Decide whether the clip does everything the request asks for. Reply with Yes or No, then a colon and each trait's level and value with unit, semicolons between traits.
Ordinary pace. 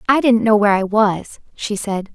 No: fast, 225 wpm